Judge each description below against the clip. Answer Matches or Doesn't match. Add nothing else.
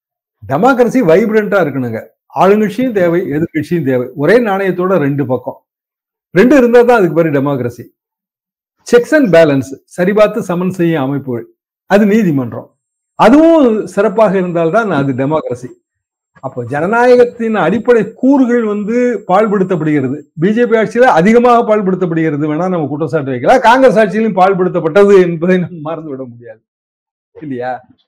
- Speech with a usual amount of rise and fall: Doesn't match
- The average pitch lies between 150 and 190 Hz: Matches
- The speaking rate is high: Doesn't match